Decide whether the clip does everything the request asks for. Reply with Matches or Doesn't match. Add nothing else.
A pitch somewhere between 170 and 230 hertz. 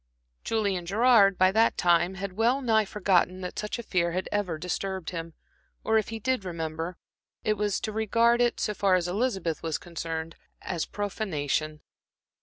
Matches